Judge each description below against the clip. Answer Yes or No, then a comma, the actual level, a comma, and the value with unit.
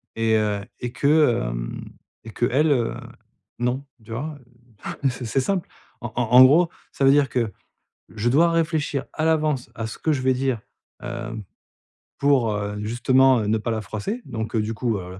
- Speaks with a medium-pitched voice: No, low, 125 Hz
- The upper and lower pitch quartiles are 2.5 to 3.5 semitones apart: No, average, 4.2 semitones